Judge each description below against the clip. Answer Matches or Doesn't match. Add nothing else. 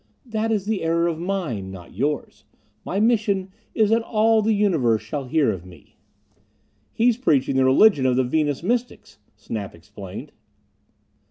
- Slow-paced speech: Doesn't match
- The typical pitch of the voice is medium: Matches